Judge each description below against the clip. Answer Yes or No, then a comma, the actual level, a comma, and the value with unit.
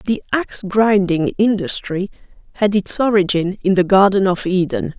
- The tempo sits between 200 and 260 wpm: No, average, 145 wpm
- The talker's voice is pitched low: No, high, 190 Hz